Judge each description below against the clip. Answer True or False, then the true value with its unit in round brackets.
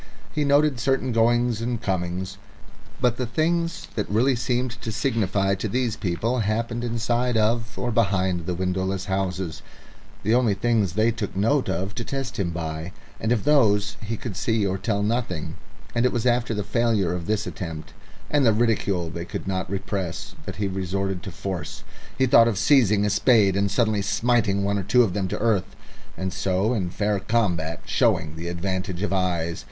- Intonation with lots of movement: False (3.9 semitones)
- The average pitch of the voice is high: False (105 Hz)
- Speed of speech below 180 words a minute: False (185 wpm)